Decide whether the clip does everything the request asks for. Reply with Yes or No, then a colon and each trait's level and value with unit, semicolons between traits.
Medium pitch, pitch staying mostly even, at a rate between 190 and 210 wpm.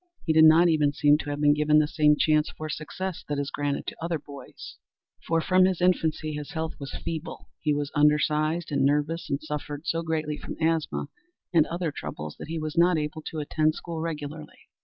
Yes: medium, 155 Hz; narrow, 1.8 semitones; fast, 205 wpm